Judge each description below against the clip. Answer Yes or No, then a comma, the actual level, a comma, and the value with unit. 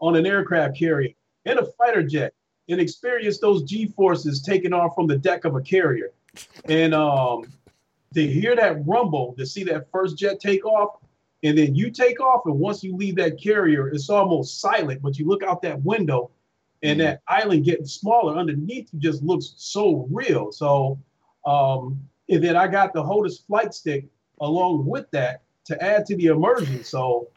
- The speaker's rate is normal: Yes, average, 185 wpm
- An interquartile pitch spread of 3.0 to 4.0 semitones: No, average, 5.2 semitones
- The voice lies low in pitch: No, medium, 165 Hz